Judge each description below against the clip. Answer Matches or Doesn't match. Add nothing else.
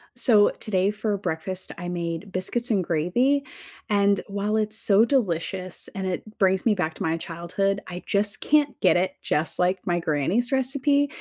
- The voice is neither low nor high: Doesn't match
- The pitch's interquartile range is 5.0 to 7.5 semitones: Doesn't match